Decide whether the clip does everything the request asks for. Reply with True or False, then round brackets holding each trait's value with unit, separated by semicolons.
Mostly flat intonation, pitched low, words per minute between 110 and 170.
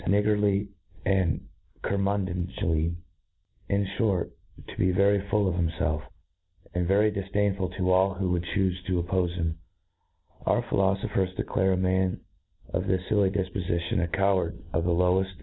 True (1.8 semitones; 95 Hz; 160 wpm)